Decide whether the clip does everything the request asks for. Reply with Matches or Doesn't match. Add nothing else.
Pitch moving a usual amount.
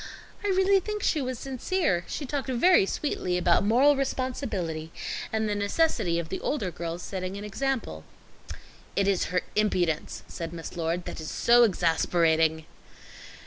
Doesn't match